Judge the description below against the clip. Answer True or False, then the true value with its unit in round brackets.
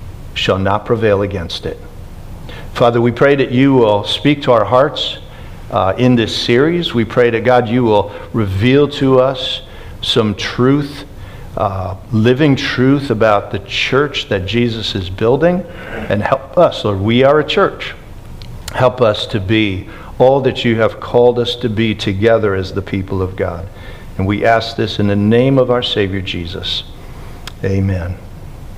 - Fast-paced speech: False (165 wpm)